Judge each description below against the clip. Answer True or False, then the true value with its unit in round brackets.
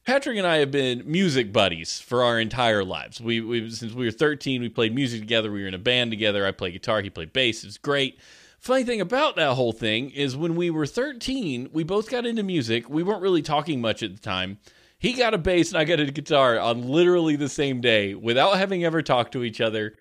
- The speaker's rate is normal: False (240 wpm)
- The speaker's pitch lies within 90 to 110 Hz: False (130 Hz)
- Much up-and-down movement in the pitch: True (7.1 semitones)